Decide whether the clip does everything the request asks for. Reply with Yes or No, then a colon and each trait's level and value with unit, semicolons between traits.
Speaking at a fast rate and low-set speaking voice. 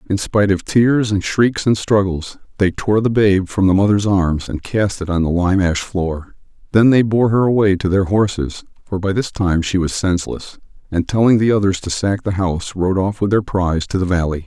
Yes: fast, 230 wpm; very low, 95 Hz